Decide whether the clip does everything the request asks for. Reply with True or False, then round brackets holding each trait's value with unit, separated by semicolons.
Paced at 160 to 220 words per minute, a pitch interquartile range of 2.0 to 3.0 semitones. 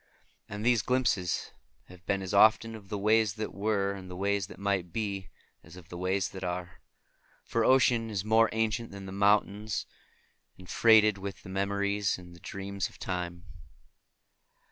True (170 wpm; 2.5 semitones)